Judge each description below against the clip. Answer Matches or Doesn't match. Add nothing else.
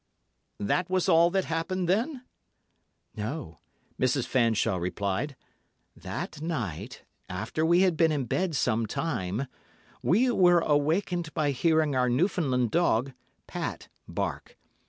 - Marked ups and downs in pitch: Matches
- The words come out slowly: Matches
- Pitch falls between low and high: Matches